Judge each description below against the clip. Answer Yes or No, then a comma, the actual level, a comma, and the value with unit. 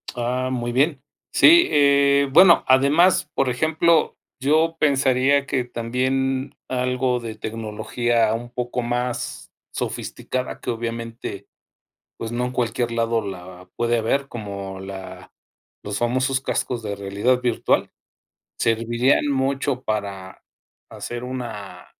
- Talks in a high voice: No, low, 125 Hz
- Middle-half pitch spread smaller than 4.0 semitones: Yes, average, 2.9 semitones